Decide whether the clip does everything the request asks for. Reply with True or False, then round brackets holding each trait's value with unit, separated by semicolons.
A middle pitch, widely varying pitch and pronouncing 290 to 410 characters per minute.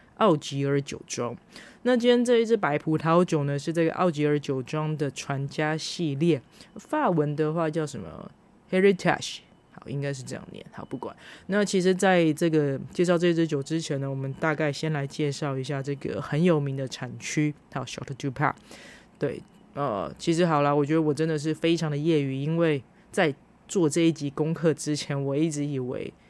False (155 Hz; 3.1 semitones; 305 characters per minute)